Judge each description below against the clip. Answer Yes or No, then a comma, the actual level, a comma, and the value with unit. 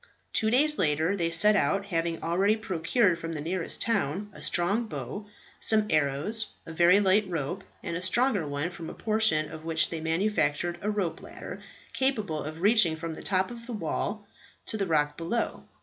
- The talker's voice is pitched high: No, medium, 180 Hz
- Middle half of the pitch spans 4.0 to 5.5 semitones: Yes, average, 4.6 semitones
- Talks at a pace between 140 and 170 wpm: No, average, 185 wpm